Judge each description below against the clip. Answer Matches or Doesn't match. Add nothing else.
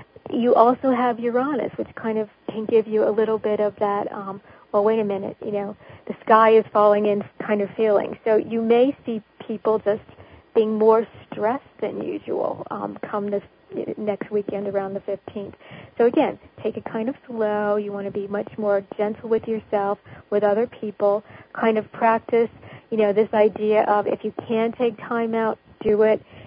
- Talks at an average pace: Matches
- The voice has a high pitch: Matches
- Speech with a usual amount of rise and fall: Doesn't match